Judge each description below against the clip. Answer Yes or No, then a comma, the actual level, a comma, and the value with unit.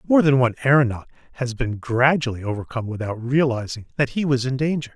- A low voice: Yes, low, 130 Hz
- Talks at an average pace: Yes, average, 180 wpm